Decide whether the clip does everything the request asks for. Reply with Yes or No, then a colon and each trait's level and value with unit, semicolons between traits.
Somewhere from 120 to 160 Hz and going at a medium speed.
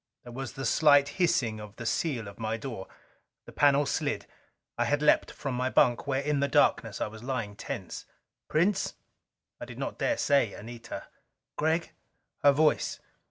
Yes: low, 135 Hz; average, 170 wpm